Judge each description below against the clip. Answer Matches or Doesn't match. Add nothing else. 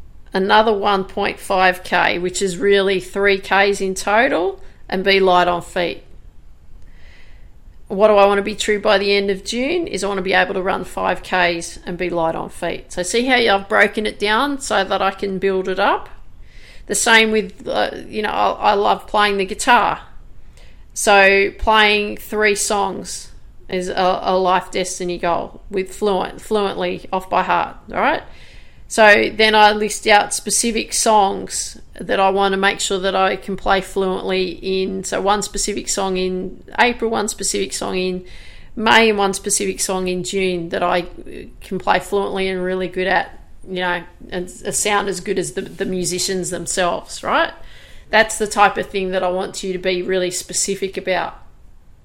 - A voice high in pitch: Matches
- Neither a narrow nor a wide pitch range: Doesn't match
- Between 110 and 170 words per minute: Doesn't match